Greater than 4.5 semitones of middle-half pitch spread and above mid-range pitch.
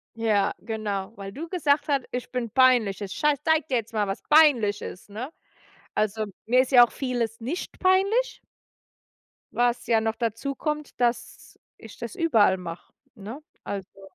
Yes: average, 5.1 semitones; high, 235 Hz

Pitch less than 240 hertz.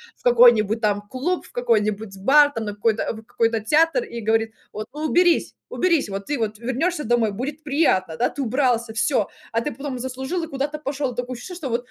No: high, 245 Hz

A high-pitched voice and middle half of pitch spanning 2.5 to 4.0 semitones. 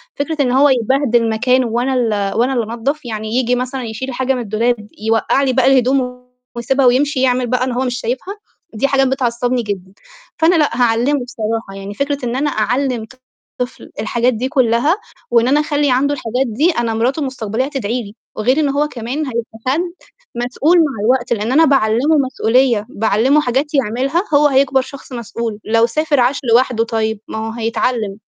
Yes: very high, 250 Hz; average, 3.0 semitones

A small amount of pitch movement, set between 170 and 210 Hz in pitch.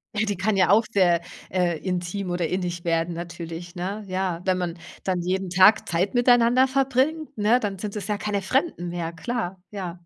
No: average, 3.5 semitones; high, 190 Hz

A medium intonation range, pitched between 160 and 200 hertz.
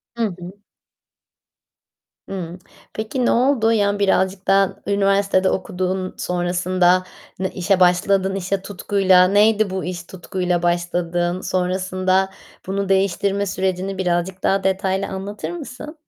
No: narrow, 1.5 semitones; high, 190 Hz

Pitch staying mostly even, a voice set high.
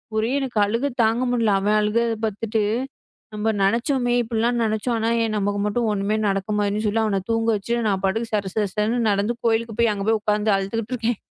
Yes: narrow, 2.0 semitones; high, 220 Hz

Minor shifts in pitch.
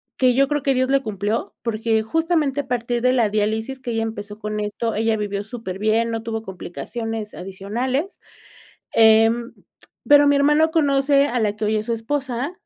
No: average, 3.9 semitones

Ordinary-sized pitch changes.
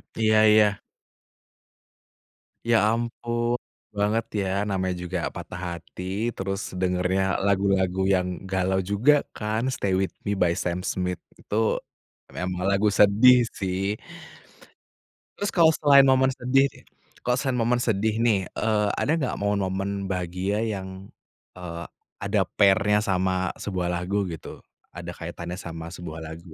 Yes: average, 3.2 semitones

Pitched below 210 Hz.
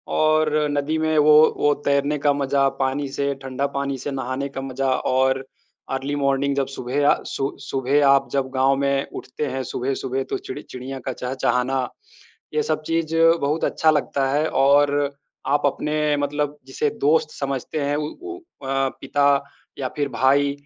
Yes: medium, 140 Hz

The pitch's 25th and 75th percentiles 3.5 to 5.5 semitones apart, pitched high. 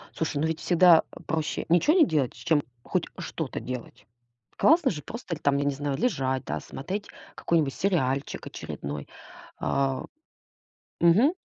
No: average, 4.8 semitones; medium, 155 Hz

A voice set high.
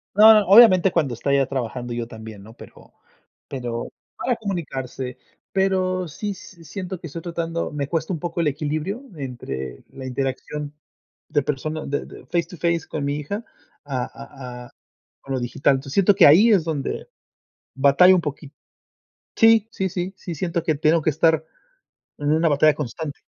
No: medium, 155 Hz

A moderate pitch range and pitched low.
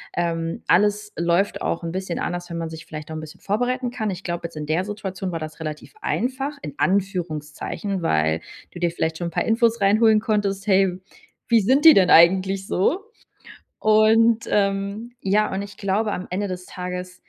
No: average, 3.8 semitones; high, 190 Hz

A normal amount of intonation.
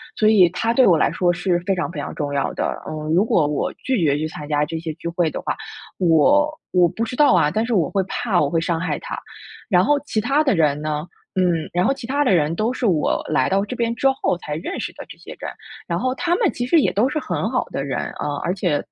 No: wide, 7.1 semitones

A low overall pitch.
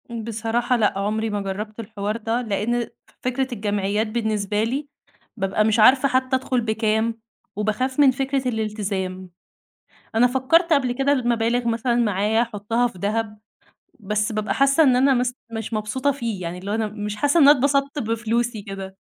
No: high, 225 Hz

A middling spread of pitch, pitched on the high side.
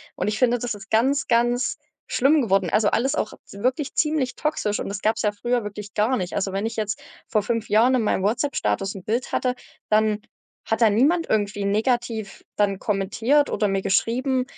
Yes: average, 3.4 semitones; high, 220 Hz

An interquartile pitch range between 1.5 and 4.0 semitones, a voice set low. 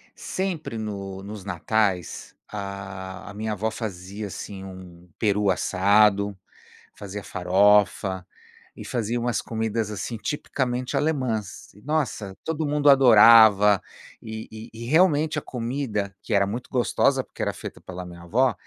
Yes: average, 3.7 semitones; low, 105 Hz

